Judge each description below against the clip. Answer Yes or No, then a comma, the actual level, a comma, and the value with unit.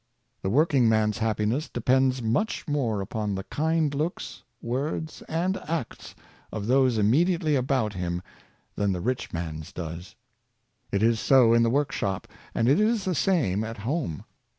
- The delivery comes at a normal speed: Yes, average, 150 wpm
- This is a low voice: Yes, low, 120 Hz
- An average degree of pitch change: No, wide, 5.9 semitones